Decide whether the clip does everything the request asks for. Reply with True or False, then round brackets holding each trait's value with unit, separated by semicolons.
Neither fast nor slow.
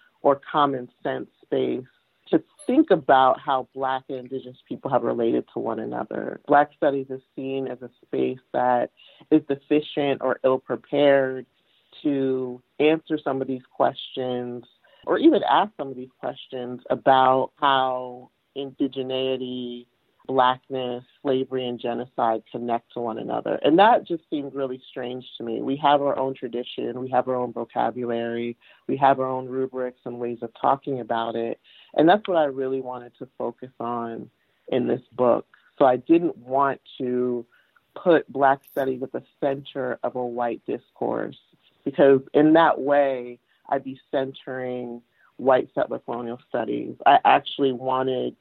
True (155 wpm)